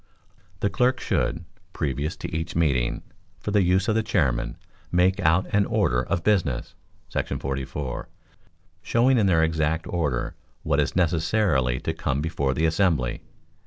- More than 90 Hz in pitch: No, very low, 80 Hz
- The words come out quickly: No, average, 150 wpm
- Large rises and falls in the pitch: Yes, wide, 5.7 semitones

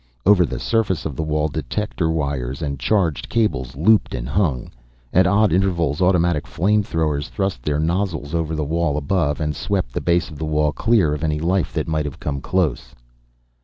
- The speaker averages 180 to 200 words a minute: Yes, average, 190 wpm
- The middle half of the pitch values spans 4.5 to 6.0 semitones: No, average, 4.1 semitones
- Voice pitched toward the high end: No, very low, 80 Hz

